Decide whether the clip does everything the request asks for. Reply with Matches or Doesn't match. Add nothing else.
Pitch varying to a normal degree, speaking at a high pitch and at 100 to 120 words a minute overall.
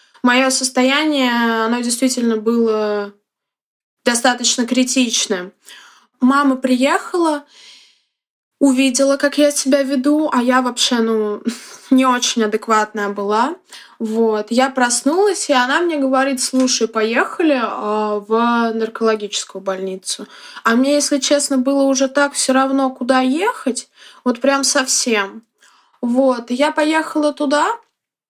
Matches